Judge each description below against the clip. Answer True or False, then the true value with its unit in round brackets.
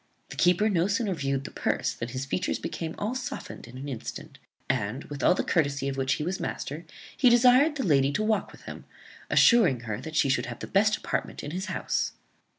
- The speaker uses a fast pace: True (220 wpm)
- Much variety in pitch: True (7.6 semitones)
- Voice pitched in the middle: True (160 Hz)